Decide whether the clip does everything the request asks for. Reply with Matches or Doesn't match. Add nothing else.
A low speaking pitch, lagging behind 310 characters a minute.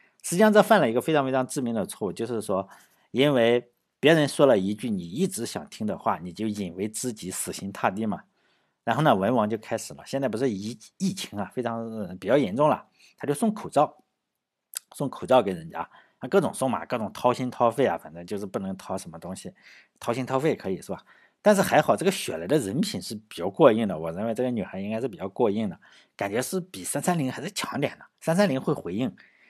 Doesn't match